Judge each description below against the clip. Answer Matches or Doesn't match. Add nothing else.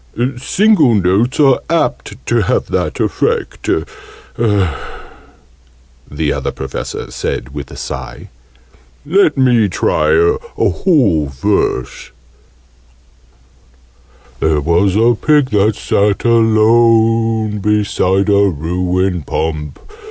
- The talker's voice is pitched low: Matches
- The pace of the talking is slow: Matches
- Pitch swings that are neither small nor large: Doesn't match